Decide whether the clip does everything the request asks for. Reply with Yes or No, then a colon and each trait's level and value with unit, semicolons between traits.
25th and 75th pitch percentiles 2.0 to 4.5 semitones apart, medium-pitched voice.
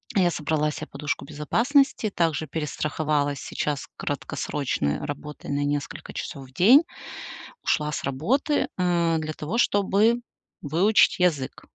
No: average, 4.9 semitones; medium, 155 Hz